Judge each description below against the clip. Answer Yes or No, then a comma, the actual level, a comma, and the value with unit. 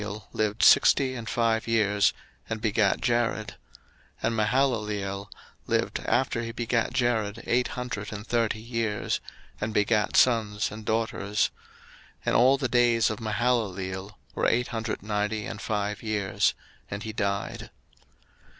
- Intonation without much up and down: Yes, narrow, 2.2 semitones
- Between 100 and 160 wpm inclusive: Yes, average, 150 wpm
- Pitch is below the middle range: Yes, low, 110 Hz